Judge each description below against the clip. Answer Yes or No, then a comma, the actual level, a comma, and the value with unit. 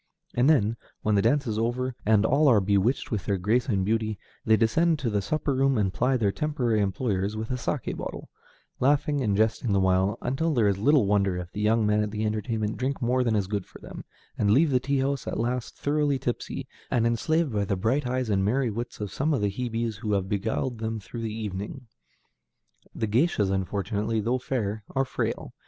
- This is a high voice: No, low, 115 Hz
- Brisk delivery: Yes, fast, 215 wpm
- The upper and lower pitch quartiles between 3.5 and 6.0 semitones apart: Yes, average, 3.9 semitones